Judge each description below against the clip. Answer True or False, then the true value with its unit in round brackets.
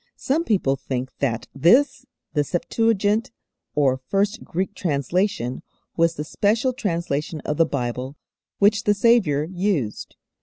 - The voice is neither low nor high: True (170 Hz)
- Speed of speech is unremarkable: False (125 wpm)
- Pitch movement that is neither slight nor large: False (6.9 semitones)